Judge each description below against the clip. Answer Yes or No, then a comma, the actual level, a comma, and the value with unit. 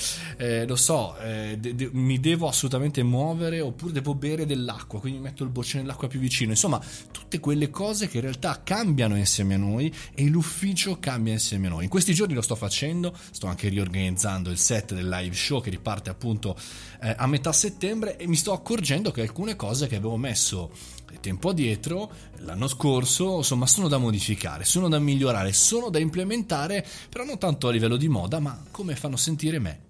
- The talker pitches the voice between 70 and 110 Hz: No, low, 135 Hz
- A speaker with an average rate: No, fast, 195 wpm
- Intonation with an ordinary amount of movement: No, wide, 6.7 semitones